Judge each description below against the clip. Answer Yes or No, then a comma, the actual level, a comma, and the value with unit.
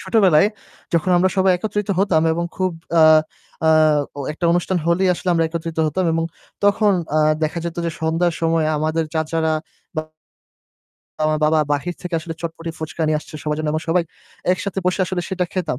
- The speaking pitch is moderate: Yes, medium, 165 Hz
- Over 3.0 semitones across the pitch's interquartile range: No, narrow, 2.6 semitones